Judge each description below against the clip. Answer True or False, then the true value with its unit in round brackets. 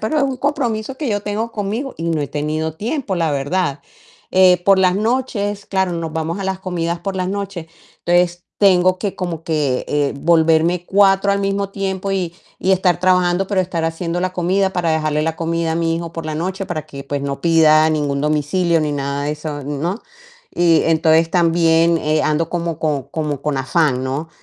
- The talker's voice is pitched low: False (170 Hz)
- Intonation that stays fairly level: False (3.5 semitones)